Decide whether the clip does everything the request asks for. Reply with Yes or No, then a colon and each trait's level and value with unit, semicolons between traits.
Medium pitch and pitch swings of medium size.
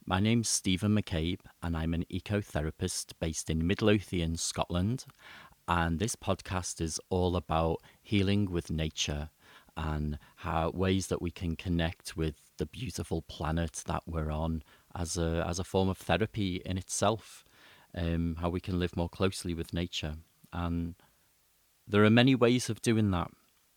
No: very low, 85 Hz; average, 3.0 semitones